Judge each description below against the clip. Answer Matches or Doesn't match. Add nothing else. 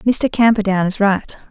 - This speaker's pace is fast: Doesn't match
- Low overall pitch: Doesn't match